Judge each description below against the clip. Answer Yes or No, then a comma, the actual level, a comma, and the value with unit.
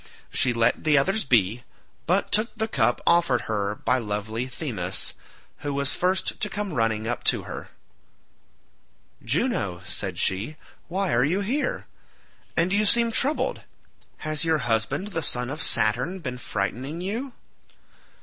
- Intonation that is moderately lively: No, wide, 8.6 semitones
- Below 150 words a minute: Yes, average, 140 wpm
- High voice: No, medium, 140 Hz